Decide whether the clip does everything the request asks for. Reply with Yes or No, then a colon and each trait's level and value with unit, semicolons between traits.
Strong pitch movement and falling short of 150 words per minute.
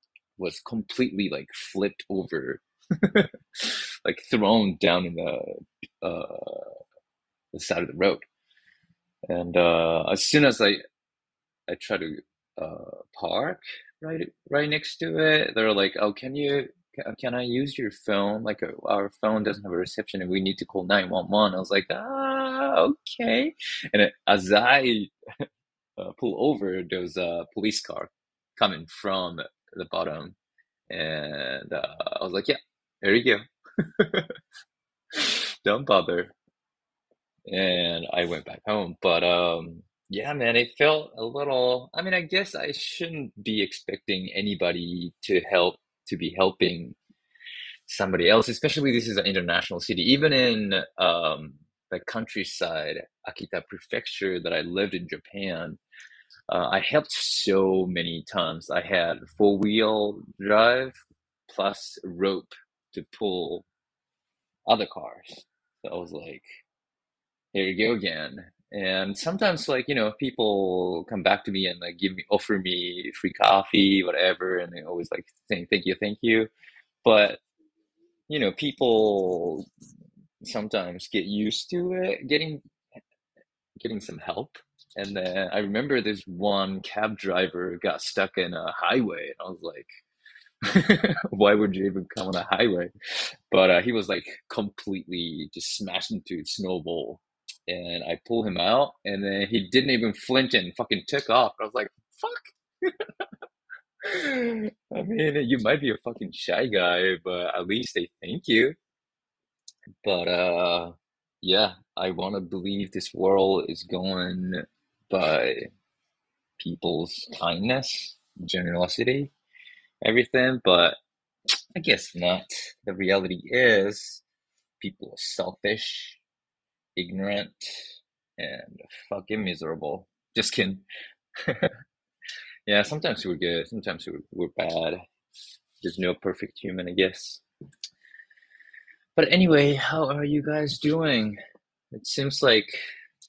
Yes: wide, 8.0 semitones; slow, 135 wpm